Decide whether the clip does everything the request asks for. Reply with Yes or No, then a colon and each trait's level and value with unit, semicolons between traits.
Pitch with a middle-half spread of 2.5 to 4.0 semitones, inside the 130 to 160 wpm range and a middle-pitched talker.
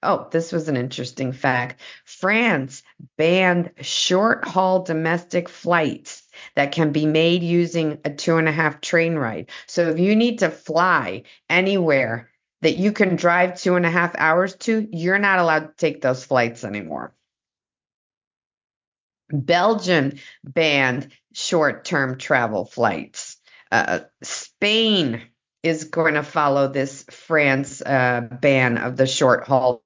No: average, 4.6 semitones; average, 140 wpm; medium, 160 Hz